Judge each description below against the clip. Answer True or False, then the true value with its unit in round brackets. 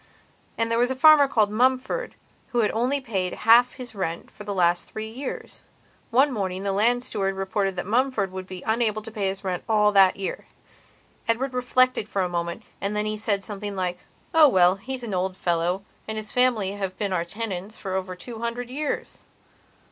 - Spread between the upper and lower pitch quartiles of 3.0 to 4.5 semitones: True (4.2 semitones)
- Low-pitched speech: False (210 Hz)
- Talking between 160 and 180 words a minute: False (200 wpm)